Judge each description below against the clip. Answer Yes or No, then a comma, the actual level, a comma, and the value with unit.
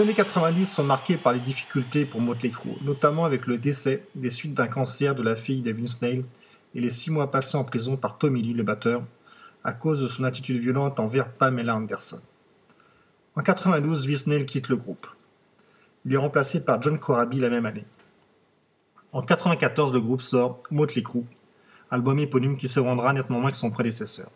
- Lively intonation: No, average, 3.3 semitones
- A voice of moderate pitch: No, low, 130 Hz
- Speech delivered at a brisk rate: No, average, 195 wpm